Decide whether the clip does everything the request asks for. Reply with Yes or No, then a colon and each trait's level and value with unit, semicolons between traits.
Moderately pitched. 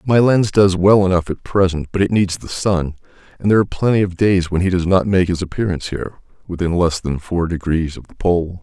No: very low, 90 Hz